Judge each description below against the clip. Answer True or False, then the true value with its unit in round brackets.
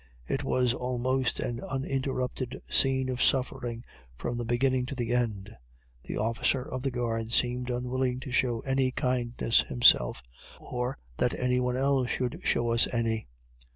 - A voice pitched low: True (125 Hz)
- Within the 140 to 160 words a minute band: True (155 wpm)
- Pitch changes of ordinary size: False (1.5 semitones)